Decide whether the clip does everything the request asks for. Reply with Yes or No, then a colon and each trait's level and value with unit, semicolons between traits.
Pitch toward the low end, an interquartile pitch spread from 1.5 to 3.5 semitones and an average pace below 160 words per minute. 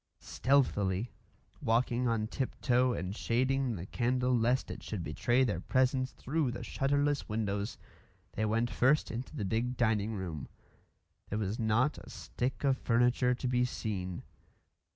Yes: low, 120 Hz; average, 3.2 semitones; average, 150 wpm